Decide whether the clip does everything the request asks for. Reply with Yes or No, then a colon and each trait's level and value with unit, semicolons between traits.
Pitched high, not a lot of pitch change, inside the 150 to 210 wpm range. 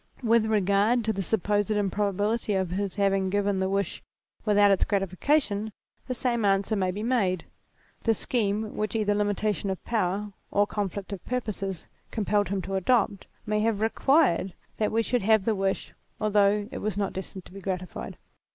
Yes: high, 205 Hz; narrow, 2.0 semitones; average, 170 wpm